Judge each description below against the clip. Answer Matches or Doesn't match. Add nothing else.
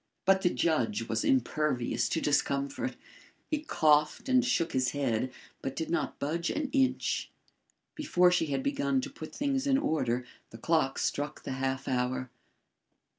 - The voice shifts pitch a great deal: Matches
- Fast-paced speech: Doesn't match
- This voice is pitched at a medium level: Matches